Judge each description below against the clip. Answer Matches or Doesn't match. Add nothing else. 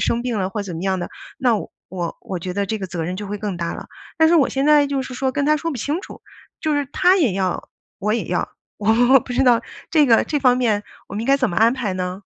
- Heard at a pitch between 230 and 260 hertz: Matches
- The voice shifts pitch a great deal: Matches